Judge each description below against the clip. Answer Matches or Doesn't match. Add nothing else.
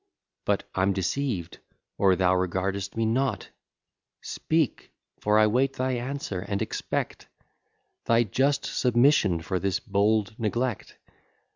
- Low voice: Matches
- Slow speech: Matches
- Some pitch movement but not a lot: Matches